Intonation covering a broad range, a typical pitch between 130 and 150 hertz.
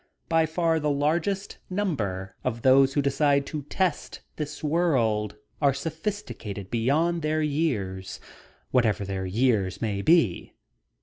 Yes: wide, 7.0 semitones; medium, 140 Hz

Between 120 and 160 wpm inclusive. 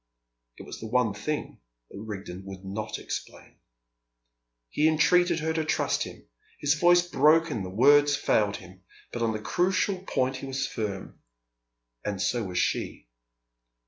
Yes: average, 155 wpm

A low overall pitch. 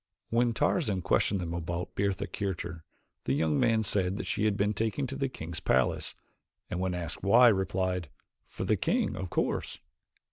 Yes: very low, 95 Hz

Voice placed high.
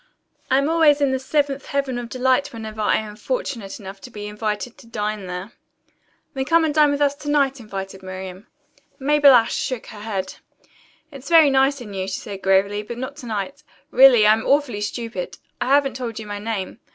Yes: high, 235 Hz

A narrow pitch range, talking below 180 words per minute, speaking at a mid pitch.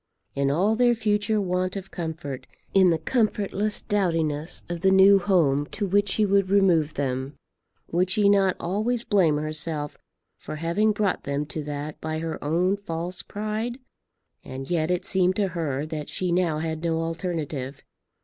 No: average, 4.4 semitones; average, 165 wpm; medium, 175 Hz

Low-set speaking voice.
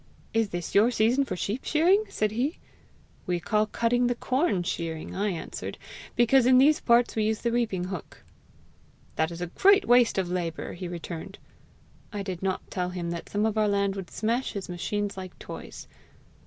No: high, 205 Hz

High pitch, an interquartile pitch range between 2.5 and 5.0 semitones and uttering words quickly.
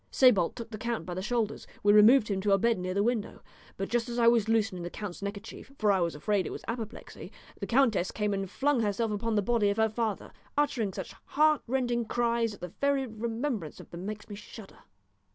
Yes: high, 220 Hz; average, 2.9 semitones; fast, 225 wpm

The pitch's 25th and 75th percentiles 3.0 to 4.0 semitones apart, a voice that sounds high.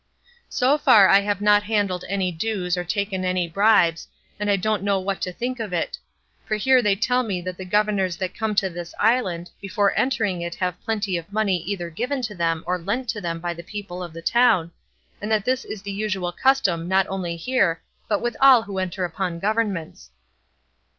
Yes: average, 3.4 semitones; high, 195 Hz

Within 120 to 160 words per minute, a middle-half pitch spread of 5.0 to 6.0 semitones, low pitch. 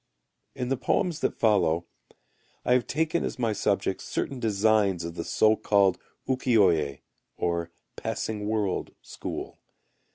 Yes: slow, 135 wpm; average, 5.3 semitones; low, 105 Hz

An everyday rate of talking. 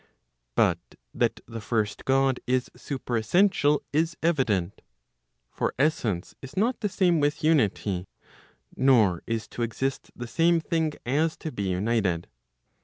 No: slow, 130 wpm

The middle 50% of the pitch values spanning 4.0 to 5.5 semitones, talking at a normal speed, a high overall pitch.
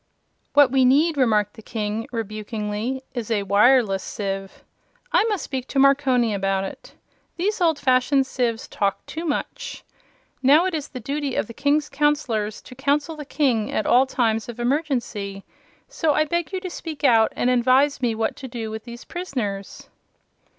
Yes: average, 4.9 semitones; average, 170 wpm; very high, 255 Hz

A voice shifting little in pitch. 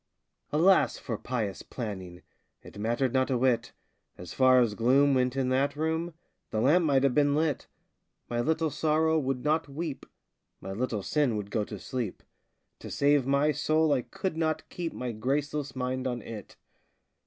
No: average, 4.1 semitones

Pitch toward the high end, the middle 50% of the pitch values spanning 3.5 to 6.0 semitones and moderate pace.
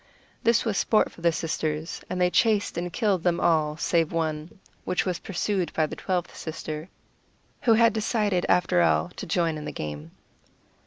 No: medium, 175 Hz; average, 3.8 semitones; average, 175 wpm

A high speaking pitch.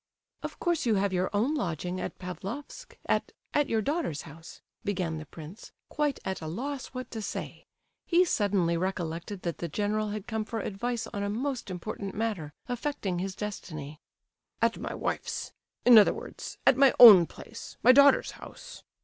Yes: high, 205 Hz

